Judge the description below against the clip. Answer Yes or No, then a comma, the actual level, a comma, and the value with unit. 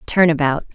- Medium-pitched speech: Yes, medium, 160 Hz